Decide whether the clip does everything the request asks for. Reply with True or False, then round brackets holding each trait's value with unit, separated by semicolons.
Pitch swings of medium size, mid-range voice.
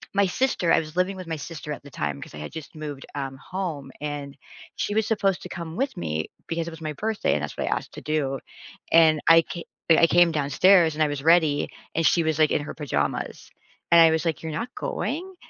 True (3.2 semitones; 160 Hz)